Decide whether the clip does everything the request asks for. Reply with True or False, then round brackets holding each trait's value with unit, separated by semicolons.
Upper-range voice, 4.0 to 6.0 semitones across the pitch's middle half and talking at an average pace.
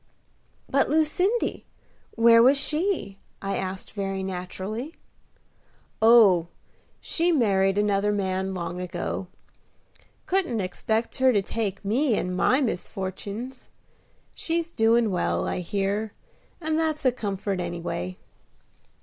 False (210 Hz; 5.4 semitones; 110 wpm)